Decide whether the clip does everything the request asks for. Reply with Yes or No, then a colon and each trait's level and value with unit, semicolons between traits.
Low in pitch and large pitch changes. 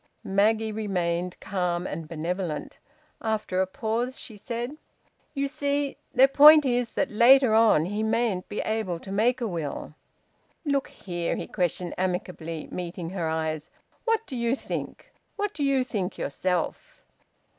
No: high, 210 Hz; wide, 5.8 semitones